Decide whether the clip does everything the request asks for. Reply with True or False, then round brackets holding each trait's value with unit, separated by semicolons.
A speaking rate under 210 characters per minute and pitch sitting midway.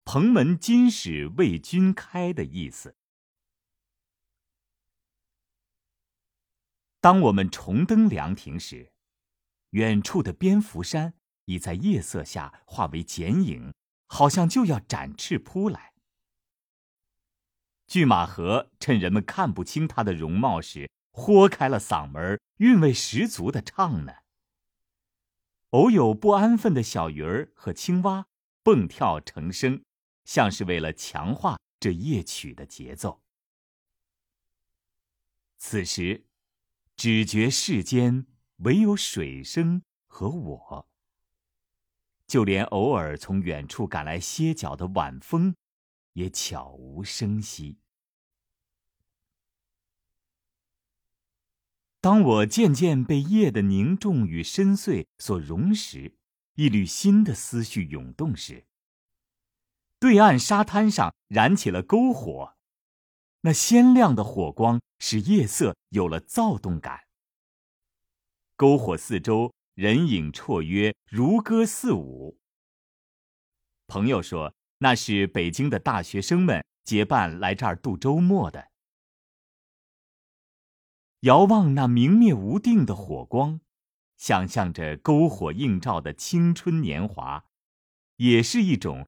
False (155 characters per minute; 105 Hz)